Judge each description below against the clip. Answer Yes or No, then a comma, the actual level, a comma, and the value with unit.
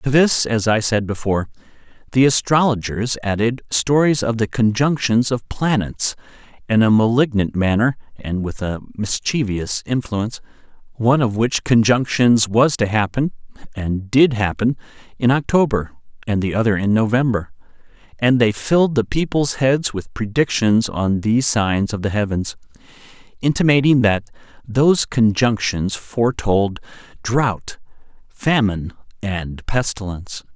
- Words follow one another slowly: Yes, slow, 125 wpm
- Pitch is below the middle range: Yes, low, 115 Hz